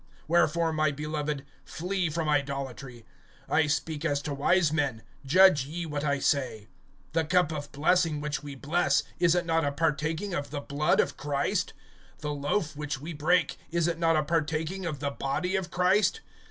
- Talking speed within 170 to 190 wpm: Yes, average, 180 wpm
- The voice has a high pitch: No, medium, 155 Hz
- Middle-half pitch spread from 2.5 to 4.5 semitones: Yes, average, 3.0 semitones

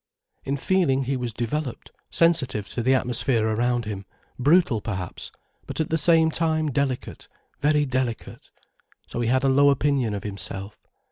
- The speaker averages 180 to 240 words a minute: No, average, 155 wpm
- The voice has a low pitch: Yes, low, 130 Hz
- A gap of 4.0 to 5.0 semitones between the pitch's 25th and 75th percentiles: Yes, average, 4.4 semitones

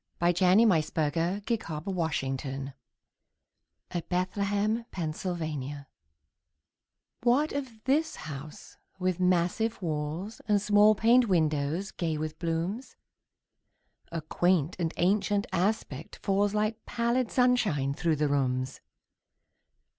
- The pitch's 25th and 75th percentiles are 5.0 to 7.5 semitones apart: Yes, wide, 5.4 semitones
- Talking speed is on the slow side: Yes, slow, 105 wpm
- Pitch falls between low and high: Yes, medium, 180 Hz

